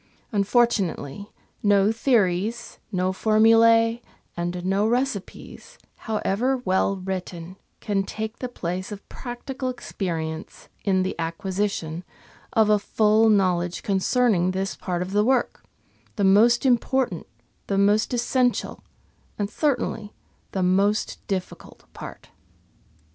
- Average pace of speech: No, slow, 115 wpm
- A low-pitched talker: No, high, 205 Hz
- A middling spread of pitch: Yes, average, 3.6 semitones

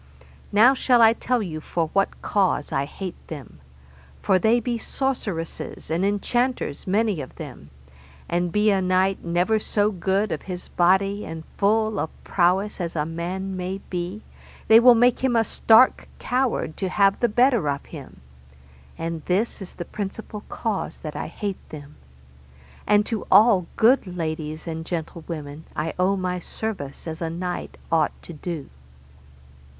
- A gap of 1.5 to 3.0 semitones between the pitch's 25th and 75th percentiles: No, average, 4.6 semitones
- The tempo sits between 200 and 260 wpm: No, average, 155 wpm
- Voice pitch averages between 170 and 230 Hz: Yes, high, 190 Hz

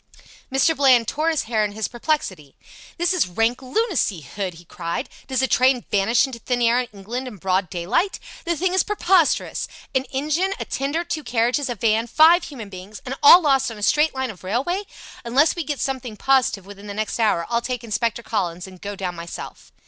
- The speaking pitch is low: No, high, 245 Hz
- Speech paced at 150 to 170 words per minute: No, fast, 205 wpm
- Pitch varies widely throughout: Yes, wide, 5.9 semitones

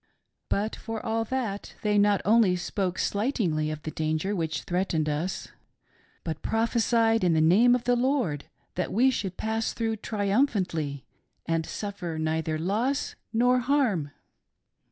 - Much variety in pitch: Yes, wide, 5.8 semitones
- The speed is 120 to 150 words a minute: Yes, average, 140 wpm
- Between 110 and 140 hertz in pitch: No, high, 200 Hz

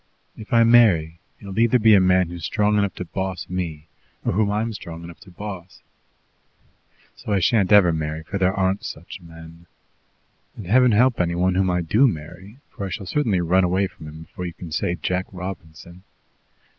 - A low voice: Yes, very low, 95 Hz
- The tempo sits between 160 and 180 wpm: No, average, 195 wpm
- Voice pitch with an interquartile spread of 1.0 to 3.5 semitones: Yes, average, 3.2 semitones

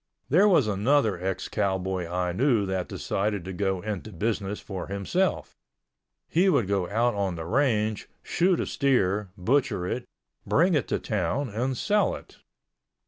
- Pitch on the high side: No, low, 105 Hz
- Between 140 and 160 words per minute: Yes, average, 155 wpm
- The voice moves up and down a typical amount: No, wide, 5.9 semitones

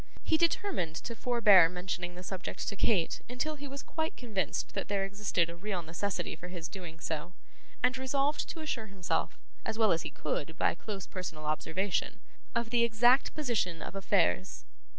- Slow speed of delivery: No, average, 175 wpm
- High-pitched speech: Yes, high, 195 Hz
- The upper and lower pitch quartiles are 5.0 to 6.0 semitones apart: Yes, wide, 5.5 semitones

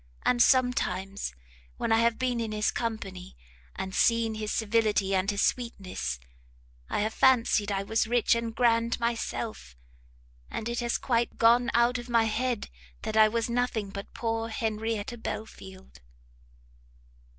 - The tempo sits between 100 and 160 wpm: Yes, average, 145 wpm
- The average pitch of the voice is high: Yes, high, 225 Hz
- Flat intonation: Yes, narrow, 2.1 semitones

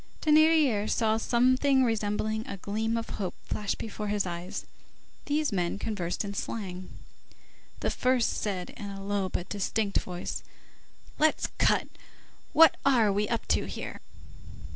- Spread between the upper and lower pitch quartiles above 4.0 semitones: No, average, 3.7 semitones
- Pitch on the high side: Yes, high, 215 Hz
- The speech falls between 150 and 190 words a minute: No, slow, 135 wpm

